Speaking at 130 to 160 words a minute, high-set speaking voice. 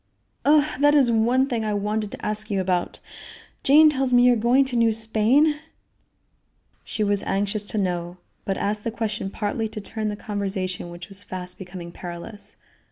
No: average, 180 wpm; high, 215 Hz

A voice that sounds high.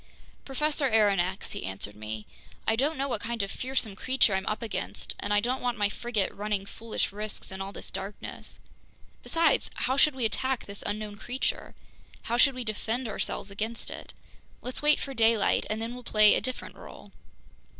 Yes: high, 225 Hz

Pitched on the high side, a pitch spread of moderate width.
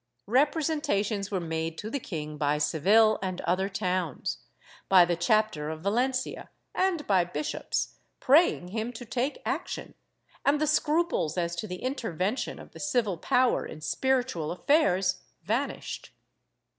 No: high, 200 Hz; wide, 6.9 semitones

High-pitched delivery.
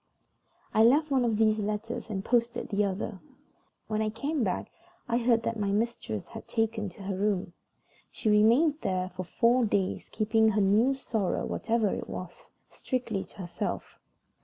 Yes: high, 215 Hz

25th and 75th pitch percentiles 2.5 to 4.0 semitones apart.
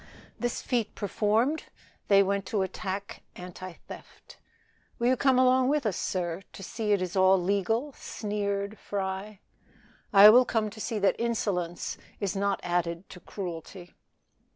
Yes: average, 2.9 semitones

